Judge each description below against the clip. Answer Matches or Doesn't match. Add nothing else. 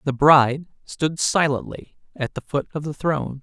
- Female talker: Doesn't match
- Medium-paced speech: Matches